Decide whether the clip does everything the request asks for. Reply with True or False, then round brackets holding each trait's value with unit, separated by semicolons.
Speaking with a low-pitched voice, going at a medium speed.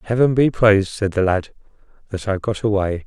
True (105 Hz; 195 wpm)